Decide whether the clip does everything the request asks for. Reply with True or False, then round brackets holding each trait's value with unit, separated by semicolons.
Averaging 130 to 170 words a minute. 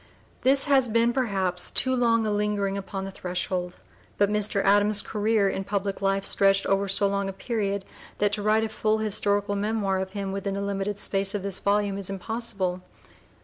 False (190 wpm)